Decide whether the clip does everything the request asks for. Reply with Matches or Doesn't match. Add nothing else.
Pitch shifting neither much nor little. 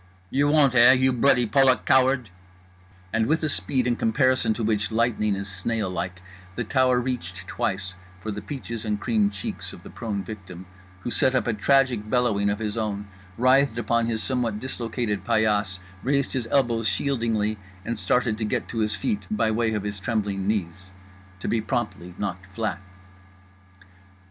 Matches